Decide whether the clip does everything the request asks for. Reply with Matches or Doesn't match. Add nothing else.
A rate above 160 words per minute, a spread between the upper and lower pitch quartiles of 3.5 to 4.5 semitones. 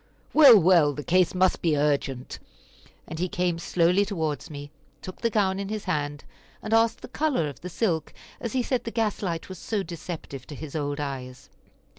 Doesn't match